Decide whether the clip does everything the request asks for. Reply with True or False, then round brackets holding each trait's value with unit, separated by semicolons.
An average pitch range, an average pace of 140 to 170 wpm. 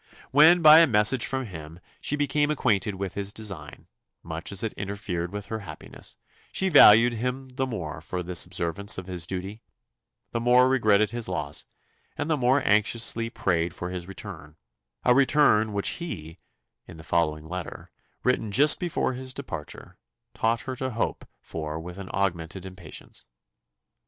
False (6.1 semitones; 160 wpm)